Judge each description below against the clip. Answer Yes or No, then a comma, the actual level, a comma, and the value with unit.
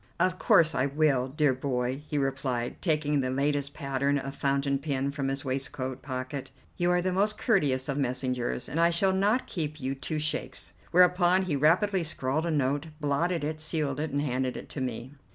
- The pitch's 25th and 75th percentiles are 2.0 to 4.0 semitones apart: Yes, average, 3.4 semitones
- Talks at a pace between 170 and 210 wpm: Yes, average, 190 wpm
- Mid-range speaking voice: Yes, medium, 145 Hz